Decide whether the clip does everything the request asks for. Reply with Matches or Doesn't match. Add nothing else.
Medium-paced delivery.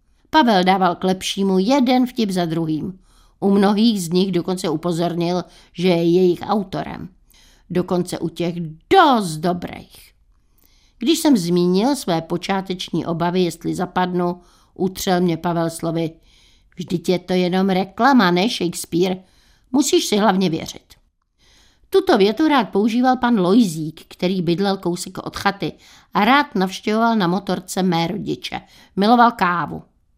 Matches